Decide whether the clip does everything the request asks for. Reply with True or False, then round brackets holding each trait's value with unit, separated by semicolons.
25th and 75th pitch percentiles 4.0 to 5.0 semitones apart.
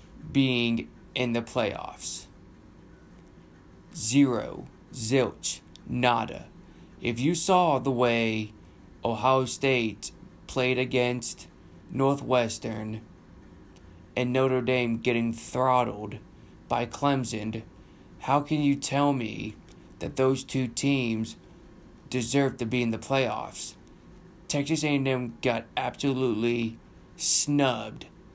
False (3.0 semitones)